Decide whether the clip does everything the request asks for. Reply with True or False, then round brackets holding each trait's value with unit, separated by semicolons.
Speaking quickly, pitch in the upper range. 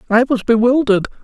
False (145 wpm; 235 Hz)